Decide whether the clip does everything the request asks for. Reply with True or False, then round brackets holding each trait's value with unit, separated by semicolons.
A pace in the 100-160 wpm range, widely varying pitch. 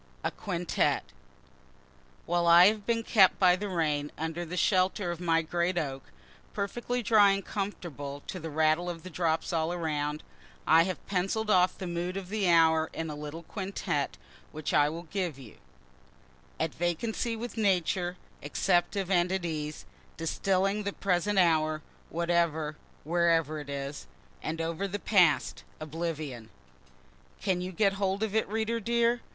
False (155 wpm; 3.7 semitones)